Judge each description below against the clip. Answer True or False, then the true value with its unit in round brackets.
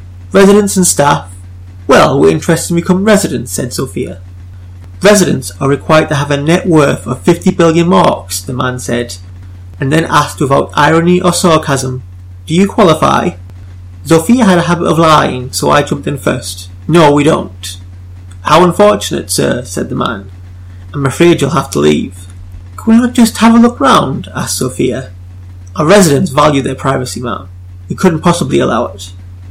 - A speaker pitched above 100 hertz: True (135 Hz)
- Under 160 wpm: False (170 wpm)